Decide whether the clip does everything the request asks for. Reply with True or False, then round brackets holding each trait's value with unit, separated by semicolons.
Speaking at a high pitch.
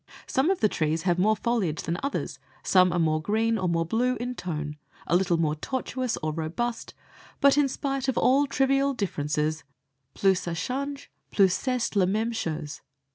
True (200 Hz)